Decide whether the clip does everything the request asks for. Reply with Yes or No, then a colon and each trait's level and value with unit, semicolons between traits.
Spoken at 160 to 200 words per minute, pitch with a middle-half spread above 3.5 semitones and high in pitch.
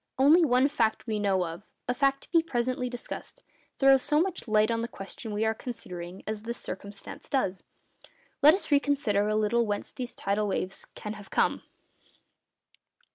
Yes: average, 165 wpm; average, 4.6 semitones; high, 225 Hz